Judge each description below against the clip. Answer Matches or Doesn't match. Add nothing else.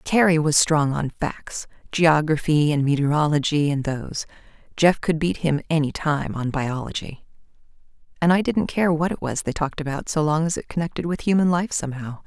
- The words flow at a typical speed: Matches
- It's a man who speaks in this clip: Doesn't match